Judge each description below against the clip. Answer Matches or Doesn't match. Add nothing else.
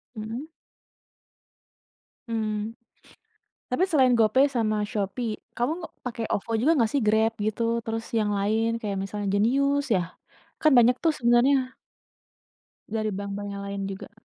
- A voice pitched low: Doesn't match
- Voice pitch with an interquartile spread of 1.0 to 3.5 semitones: Matches